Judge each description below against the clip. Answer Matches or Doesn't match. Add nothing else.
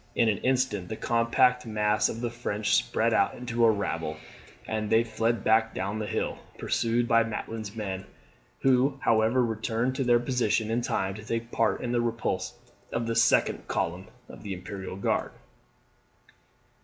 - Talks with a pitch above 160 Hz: Doesn't match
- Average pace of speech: Matches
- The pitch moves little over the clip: Matches